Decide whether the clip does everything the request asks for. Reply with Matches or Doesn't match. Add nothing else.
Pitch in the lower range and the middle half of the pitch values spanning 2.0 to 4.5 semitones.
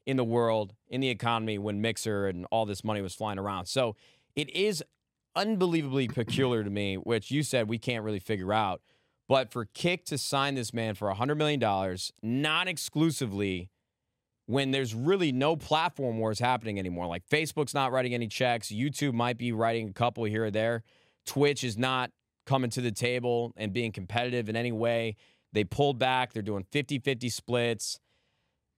Matches